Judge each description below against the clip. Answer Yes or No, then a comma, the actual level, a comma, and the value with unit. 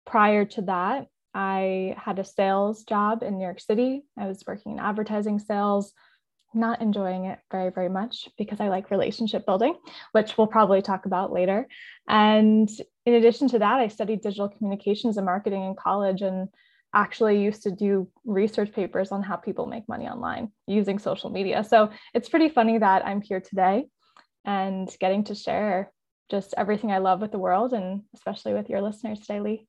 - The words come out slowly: No, average, 180 wpm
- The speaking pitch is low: No, high, 205 Hz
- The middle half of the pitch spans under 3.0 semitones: Yes, narrow, 2.5 semitones